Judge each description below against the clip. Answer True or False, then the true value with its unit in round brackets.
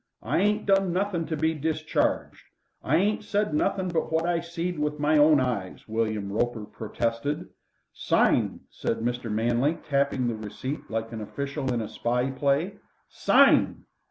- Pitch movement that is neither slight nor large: False (6.2 semitones)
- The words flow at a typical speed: True (155 wpm)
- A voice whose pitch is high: False (145 Hz)